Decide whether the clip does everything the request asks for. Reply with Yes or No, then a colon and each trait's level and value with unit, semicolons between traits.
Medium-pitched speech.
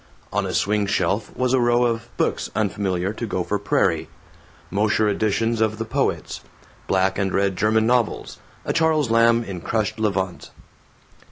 No: low, 110 Hz